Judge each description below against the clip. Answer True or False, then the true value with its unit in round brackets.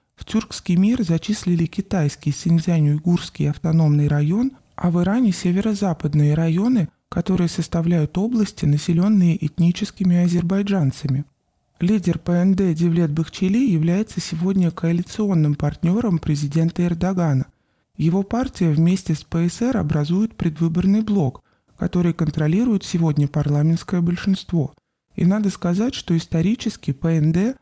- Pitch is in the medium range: True (175 Hz)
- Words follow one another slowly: True (105 wpm)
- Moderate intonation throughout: True (3.3 semitones)